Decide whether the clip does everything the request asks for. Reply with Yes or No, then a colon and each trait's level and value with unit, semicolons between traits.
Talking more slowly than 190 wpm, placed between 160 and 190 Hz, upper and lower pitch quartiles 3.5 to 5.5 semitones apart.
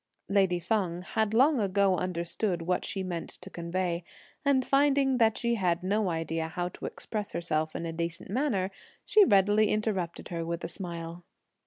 Yes: average, 170 wpm; medium, 185 Hz; average, 4.1 semitones